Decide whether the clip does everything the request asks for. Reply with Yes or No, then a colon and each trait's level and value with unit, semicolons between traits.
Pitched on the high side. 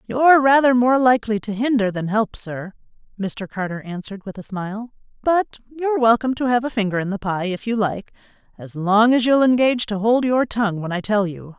Yes: high, 220 Hz